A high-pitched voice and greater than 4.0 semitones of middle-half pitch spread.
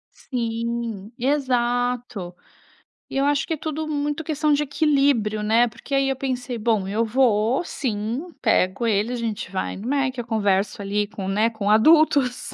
Yes: high, 240 Hz; average, 4.4 semitones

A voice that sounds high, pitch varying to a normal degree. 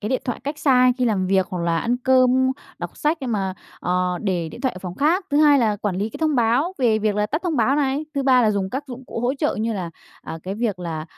No: high, 235 Hz; wide, 5.8 semitones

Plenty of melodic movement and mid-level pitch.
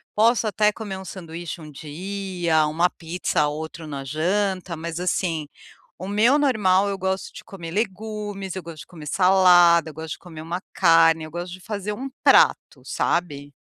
No: average, 3.5 semitones; medium, 180 Hz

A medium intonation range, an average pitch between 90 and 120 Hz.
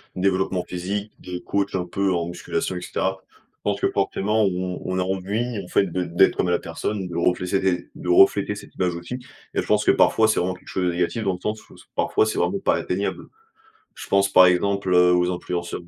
No: narrow, 2.0 semitones; very low, 95 Hz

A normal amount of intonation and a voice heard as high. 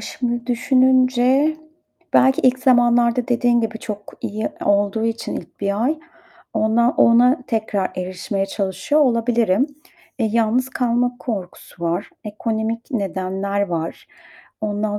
Yes: average, 3.4 semitones; high, 230 Hz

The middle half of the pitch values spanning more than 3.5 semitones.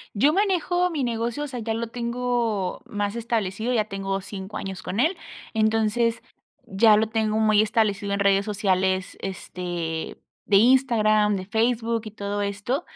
No: average, 2.9 semitones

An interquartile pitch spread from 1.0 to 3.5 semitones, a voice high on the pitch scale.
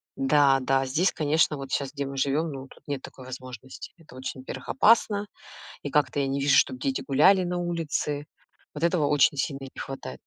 No: narrow, 2.5 semitones; medium, 140 Hz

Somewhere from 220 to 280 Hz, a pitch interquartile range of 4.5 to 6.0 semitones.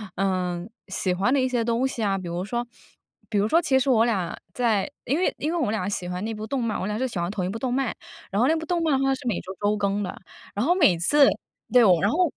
Yes: high, 225 Hz; wide, 5.4 semitones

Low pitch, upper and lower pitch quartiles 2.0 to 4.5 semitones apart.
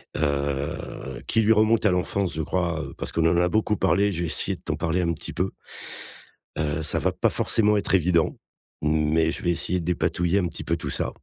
Yes: very low, 85 Hz; average, 3.3 semitones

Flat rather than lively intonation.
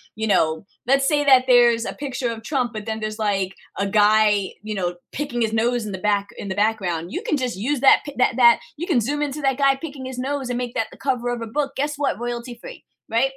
No: average, 4.1 semitones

